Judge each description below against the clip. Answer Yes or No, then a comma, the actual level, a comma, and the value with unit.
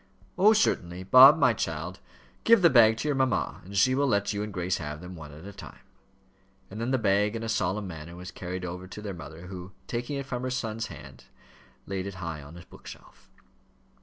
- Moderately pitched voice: No, low, 100 Hz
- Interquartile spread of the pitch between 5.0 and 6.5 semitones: Yes, wide, 5.5 semitones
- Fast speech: Yes, fast, 220 wpm